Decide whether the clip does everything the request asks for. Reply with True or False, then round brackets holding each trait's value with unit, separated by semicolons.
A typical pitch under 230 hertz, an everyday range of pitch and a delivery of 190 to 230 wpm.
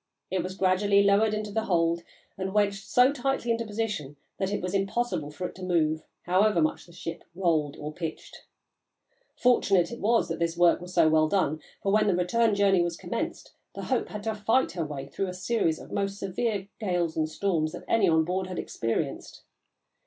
True (190 Hz; 3.8 semitones; 200 wpm)